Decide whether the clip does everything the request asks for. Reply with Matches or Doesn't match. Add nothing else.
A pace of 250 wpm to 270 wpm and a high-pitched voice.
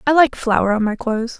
Matches